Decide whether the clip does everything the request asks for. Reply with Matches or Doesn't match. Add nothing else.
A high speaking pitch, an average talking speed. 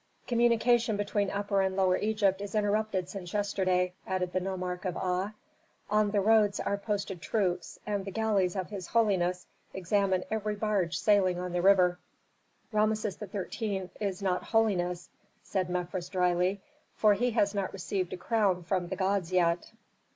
Matches